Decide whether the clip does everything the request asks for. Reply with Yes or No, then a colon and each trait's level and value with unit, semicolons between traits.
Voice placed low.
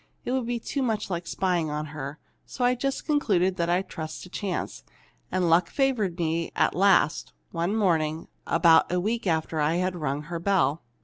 No: medium, 175 Hz